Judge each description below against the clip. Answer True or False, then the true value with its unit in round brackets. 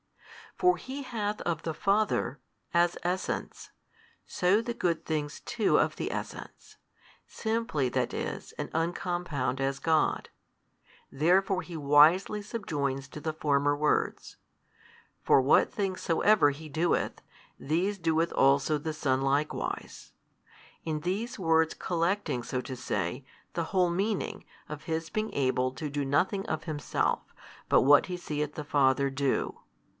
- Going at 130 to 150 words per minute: True (140 wpm)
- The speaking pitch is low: False (160 Hz)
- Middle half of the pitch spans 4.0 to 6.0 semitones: True (4.7 semitones)